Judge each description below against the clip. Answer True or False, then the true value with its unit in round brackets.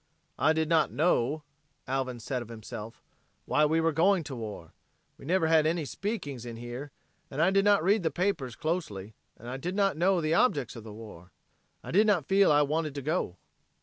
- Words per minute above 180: True (200 wpm)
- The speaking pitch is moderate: True (155 Hz)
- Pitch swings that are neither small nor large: False (6.2 semitones)